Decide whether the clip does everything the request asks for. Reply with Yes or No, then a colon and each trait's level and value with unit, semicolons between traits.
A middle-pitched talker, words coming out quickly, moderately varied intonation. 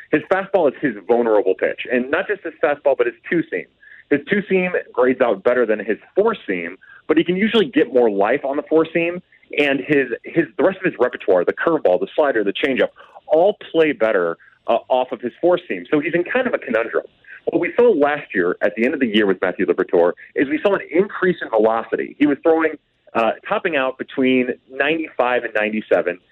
No: medium, 165 Hz; fast, 215 wpm; wide, 8.4 semitones